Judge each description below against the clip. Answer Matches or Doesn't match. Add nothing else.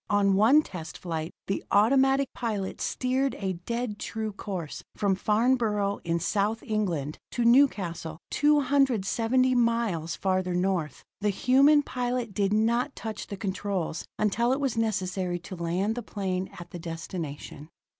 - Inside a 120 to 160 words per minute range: Matches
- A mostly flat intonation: Doesn't match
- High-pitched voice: Matches